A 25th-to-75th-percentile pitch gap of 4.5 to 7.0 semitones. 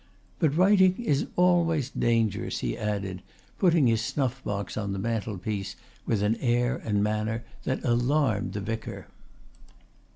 Yes: average, 5.3 semitones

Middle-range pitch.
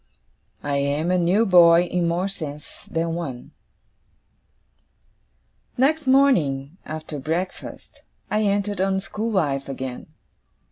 Yes: medium, 170 Hz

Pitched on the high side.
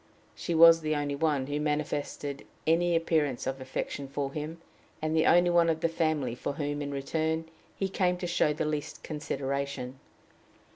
No: medium, 150 Hz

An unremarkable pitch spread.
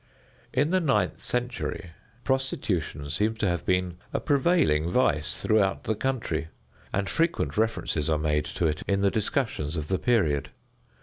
No: wide, 8.0 semitones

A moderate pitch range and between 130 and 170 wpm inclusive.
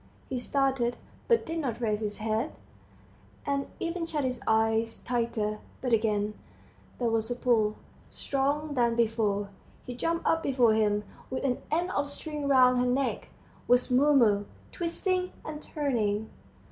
Yes: average, 4.4 semitones; average, 145 wpm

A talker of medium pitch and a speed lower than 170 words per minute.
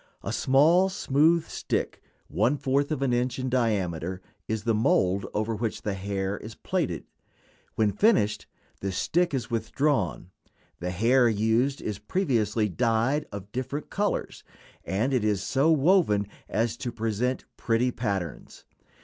No: low, 115 Hz; average, 140 wpm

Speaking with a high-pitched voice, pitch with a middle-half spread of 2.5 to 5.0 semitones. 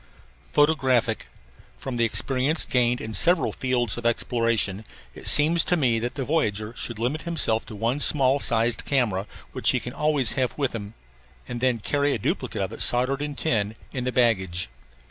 No: low, 125 Hz; average, 3.8 semitones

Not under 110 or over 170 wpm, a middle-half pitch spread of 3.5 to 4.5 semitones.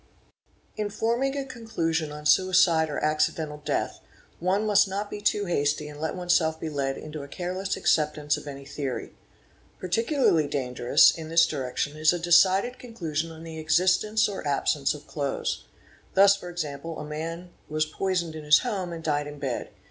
No: average, 180 wpm; average, 4.1 semitones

